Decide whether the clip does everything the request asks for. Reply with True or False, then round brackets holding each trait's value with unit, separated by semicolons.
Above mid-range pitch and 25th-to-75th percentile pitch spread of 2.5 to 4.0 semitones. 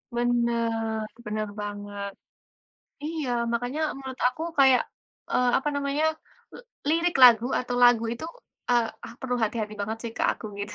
True (240 Hz; 3.2 semitones)